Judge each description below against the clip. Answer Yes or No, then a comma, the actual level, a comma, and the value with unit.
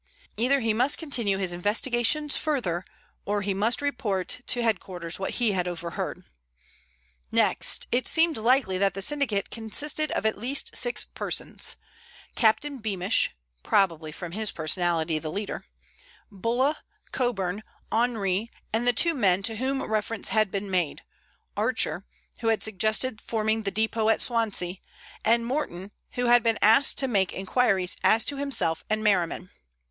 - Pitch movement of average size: Yes, average, 4.3 semitones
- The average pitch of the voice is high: Yes, high, 220 Hz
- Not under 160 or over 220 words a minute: No, average, 150 wpm